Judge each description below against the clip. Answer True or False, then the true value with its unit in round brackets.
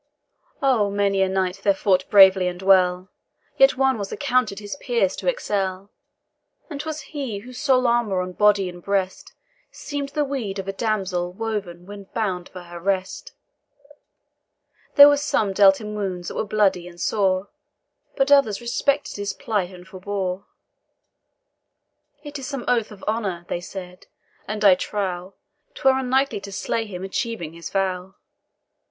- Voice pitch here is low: False (200 Hz)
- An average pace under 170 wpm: True (155 wpm)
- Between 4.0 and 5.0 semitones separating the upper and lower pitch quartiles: True (4.3 semitones)